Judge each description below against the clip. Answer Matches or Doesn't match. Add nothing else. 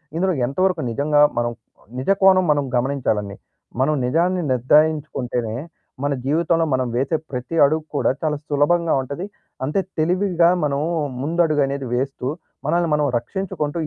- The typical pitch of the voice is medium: Matches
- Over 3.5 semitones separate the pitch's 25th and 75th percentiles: Matches